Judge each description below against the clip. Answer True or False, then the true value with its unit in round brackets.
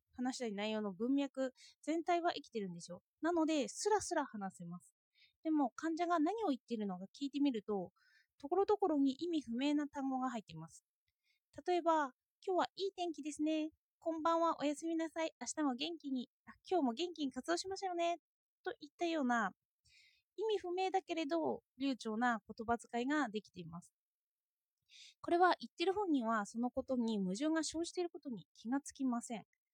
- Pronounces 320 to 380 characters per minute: True (355 characters per minute)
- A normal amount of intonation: False (6.1 semitones)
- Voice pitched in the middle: False (290 Hz)